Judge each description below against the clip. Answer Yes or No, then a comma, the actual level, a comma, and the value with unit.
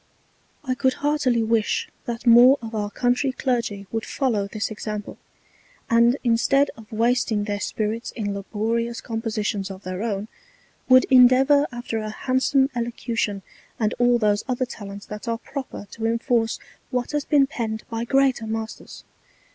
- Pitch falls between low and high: No, high, 230 Hz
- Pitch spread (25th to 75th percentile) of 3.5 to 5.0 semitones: No, average, 2.9 semitones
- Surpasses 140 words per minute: Yes, average, 155 wpm